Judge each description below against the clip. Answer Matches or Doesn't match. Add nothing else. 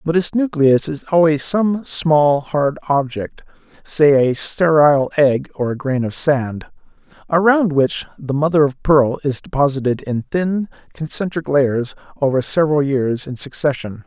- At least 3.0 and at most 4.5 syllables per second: Matches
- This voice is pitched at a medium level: Matches